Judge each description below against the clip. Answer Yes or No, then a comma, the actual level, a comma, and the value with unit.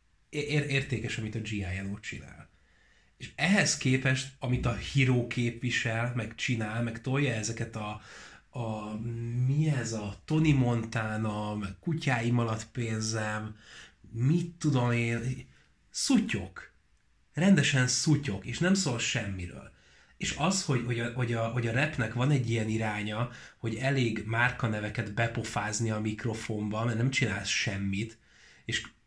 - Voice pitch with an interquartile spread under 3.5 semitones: Yes, average, 3.0 semitones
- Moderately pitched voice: No, low, 115 Hz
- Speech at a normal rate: Yes, average, 130 wpm